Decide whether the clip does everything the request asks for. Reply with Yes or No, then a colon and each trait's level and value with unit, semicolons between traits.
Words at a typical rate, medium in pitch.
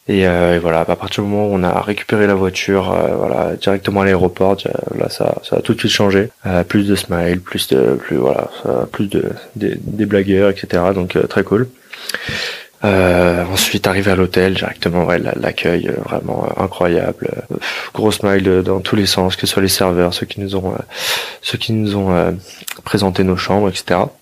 No: average, 210 wpm; very low, 95 Hz